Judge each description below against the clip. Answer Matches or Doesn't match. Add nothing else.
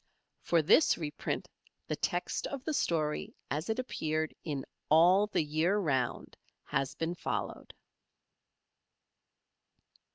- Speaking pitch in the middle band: Matches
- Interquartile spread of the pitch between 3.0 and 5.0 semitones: Matches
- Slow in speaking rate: Matches